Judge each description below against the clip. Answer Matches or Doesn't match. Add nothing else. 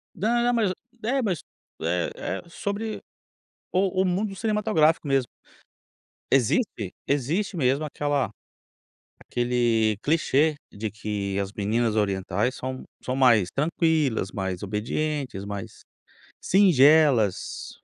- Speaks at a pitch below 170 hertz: Matches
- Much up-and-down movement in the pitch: Matches